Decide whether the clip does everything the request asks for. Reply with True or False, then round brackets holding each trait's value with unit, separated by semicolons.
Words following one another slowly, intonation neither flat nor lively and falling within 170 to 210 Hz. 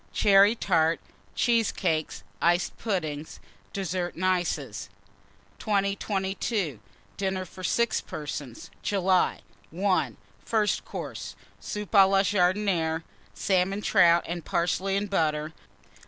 True (100 wpm; 3.1 semitones; 185 Hz)